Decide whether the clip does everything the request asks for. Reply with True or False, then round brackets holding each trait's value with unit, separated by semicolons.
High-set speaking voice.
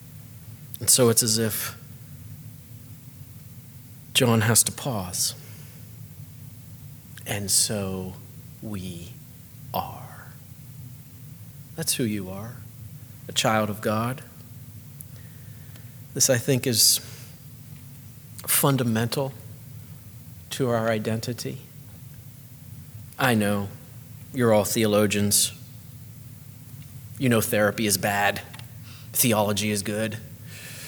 False (125 Hz)